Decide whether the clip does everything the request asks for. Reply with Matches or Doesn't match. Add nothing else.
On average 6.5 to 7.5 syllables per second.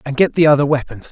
Matches